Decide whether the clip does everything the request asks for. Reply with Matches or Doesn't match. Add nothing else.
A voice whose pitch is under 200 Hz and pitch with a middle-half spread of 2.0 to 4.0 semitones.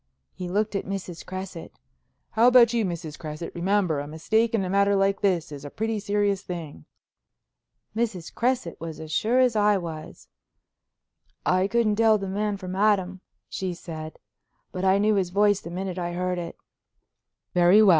Matches